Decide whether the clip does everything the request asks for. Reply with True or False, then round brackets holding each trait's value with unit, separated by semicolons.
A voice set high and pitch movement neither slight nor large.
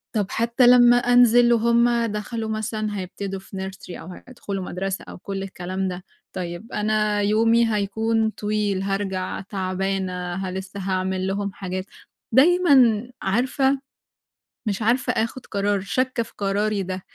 True (205 Hz; 3.3 semitones)